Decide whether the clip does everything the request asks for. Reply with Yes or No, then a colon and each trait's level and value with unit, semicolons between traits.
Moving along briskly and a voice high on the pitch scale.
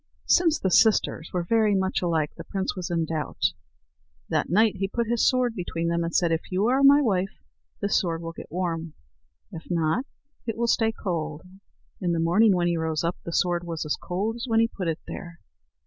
No: fast, 215 wpm; medium, 180 Hz